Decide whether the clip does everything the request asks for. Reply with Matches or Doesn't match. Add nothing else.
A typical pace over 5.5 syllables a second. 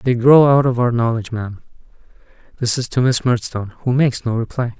Matches